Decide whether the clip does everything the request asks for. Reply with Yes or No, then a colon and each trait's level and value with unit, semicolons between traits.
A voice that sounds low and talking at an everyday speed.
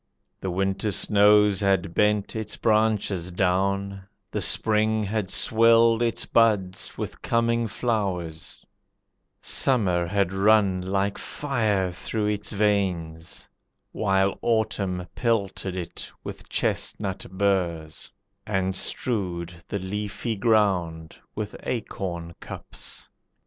No: low, 100 Hz; slow, 100 wpm